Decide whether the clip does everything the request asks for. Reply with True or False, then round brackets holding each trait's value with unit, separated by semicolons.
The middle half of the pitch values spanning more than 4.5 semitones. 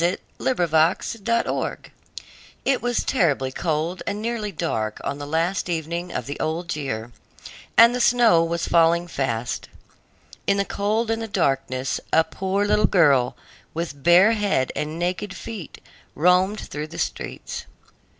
True (5.3 semitones)